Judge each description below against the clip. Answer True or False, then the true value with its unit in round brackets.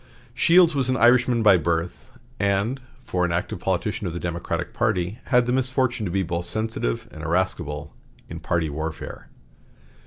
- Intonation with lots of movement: True (6.1 semitones)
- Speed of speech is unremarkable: True (160 wpm)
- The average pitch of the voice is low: True (95 Hz)